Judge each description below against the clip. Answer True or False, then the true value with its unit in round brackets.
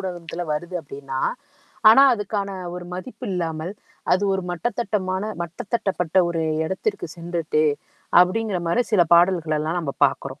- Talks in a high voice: False (180 Hz)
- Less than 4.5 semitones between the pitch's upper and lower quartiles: True (3.0 semitones)